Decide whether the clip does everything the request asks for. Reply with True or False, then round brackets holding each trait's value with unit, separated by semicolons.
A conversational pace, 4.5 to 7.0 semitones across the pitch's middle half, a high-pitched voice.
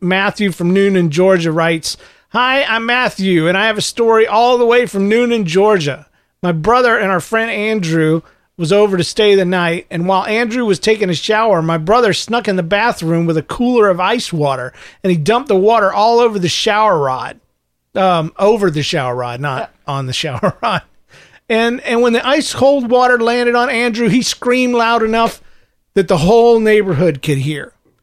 True (195 wpm; 5.2 semitones; 205 Hz)